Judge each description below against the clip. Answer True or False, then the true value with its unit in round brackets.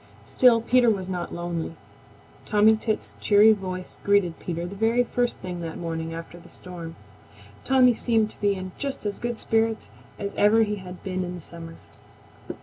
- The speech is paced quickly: False (170 wpm)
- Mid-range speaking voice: False (200 Hz)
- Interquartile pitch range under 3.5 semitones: False (4.2 semitones)